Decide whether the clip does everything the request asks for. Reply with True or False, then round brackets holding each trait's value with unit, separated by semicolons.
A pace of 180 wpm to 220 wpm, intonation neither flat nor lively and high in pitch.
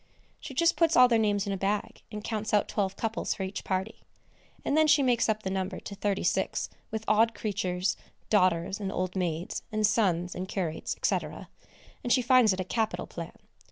True (200 wpm; 3.0 semitones; 205 Hz)